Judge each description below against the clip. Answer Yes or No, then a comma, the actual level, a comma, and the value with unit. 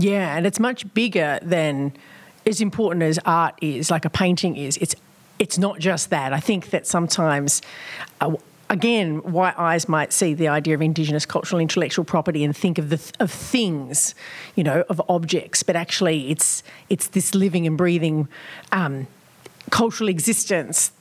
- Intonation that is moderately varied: Yes, average, 3.6 semitones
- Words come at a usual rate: Yes, average, 170 wpm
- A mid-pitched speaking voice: Yes, medium, 175 Hz